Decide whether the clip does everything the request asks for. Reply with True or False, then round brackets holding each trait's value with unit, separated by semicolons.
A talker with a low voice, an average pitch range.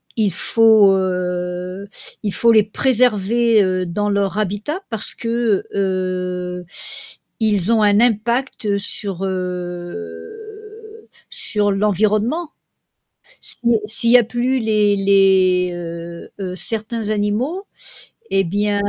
False (205 Hz; 3.7 semitones)